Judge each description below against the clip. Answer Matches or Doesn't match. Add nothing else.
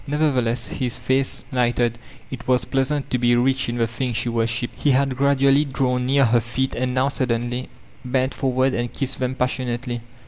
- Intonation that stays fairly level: Matches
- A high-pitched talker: Doesn't match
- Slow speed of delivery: Doesn't match